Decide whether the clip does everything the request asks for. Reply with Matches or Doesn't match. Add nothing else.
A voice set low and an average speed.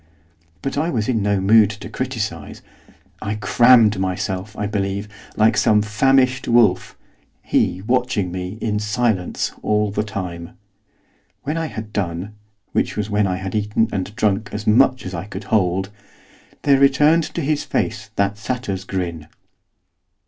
Matches